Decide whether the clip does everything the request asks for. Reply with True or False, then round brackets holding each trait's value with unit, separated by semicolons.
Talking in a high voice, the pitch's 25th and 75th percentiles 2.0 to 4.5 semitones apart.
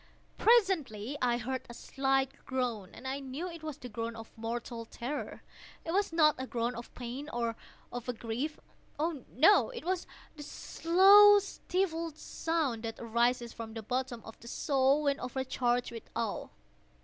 False (260 Hz; 4.9 semitones)